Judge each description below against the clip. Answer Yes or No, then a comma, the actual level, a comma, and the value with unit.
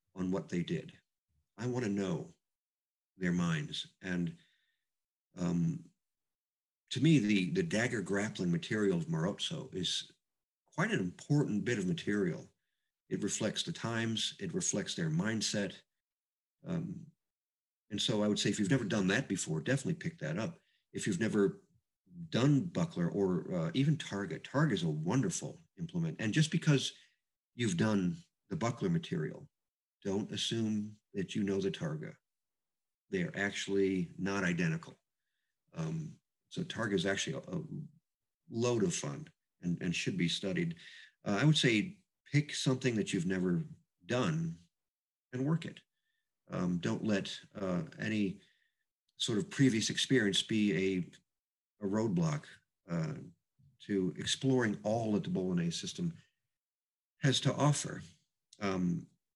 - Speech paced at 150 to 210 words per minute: No, average, 140 wpm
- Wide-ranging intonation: Yes, wide, 9.0 semitones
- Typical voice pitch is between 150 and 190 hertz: No, low, 135 Hz